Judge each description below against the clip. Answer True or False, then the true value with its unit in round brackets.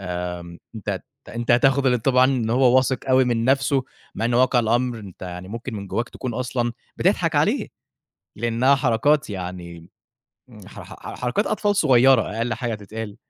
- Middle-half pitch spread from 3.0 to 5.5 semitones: True (3.4 semitones)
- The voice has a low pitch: True (120 Hz)